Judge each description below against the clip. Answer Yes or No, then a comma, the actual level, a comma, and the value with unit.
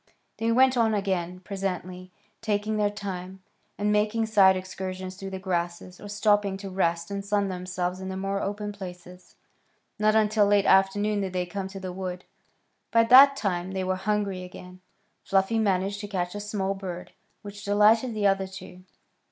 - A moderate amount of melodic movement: No, narrow, 2.0 semitones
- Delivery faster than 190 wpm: No, average, 175 wpm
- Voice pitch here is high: Yes, high, 195 Hz